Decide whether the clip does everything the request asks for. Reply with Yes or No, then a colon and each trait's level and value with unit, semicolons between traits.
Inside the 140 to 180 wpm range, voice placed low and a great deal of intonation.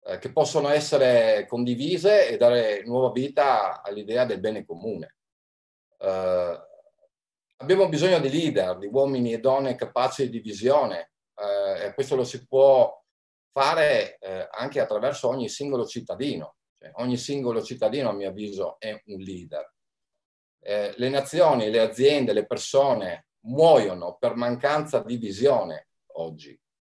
No: average, 130 wpm; low, 125 Hz; wide, 6.4 semitones